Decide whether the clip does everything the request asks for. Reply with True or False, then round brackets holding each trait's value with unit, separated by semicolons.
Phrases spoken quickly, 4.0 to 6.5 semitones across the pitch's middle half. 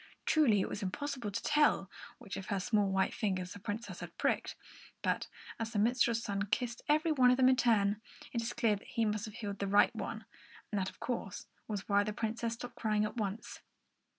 False (215 wpm; 2.9 semitones)